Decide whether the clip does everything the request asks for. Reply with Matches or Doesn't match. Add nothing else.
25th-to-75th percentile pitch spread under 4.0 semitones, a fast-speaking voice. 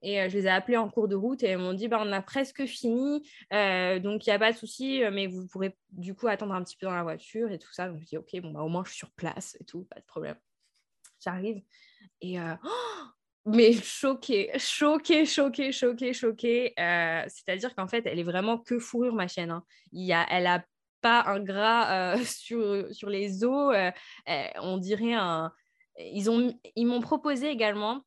Doesn't match